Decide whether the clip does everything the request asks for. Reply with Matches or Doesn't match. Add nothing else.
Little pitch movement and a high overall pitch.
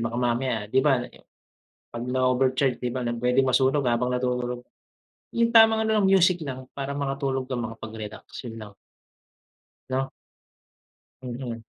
Doesn't match